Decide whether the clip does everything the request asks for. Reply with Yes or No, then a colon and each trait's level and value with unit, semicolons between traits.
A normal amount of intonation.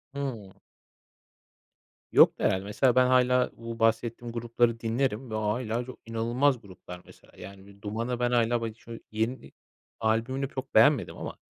No: narrow, 2.3 semitones